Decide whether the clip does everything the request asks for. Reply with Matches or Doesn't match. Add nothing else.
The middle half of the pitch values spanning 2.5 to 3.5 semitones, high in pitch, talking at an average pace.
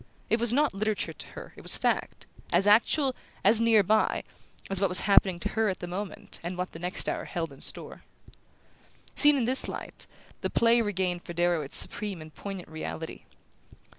Doesn't match